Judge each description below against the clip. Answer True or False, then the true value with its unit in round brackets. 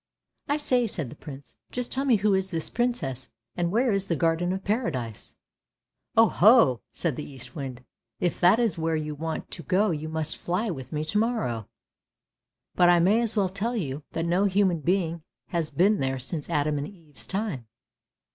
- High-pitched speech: False (170 Hz)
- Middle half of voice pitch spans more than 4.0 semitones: True (5.5 semitones)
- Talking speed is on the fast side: True (210 wpm)